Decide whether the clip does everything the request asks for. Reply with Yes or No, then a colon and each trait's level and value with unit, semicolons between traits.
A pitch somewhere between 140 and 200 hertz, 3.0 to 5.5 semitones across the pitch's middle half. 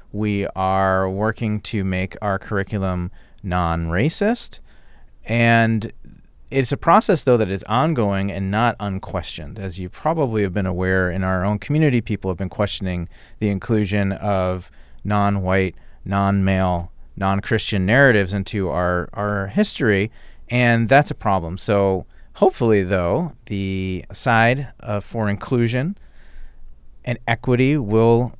No: low, 100 Hz; average, 3.6 semitones